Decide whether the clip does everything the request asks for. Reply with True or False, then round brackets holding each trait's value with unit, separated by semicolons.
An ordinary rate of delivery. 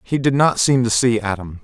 False (255 wpm)